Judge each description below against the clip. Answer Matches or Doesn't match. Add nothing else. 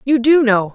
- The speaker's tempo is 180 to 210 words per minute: Doesn't match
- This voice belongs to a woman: Matches